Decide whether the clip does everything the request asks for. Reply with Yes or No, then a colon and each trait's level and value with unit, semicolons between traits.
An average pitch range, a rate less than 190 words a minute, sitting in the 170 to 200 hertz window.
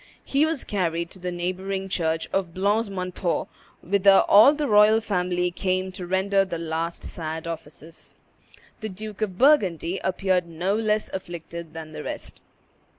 Yes: average, 3.0 semitones; average, 150 wpm; medium, 185 Hz